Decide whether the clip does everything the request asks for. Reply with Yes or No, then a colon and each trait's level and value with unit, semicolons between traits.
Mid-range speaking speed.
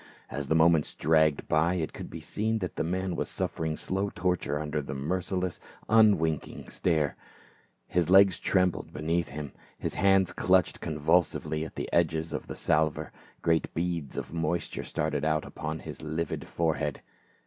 Yes: average, 165 wpm